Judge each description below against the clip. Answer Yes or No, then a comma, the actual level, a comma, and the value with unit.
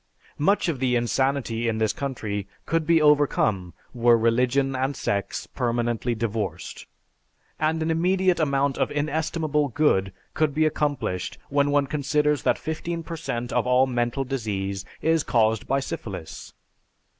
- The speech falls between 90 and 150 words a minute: Yes, average, 145 wpm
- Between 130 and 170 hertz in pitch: Yes, low, 135 Hz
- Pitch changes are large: No, average, 4.6 semitones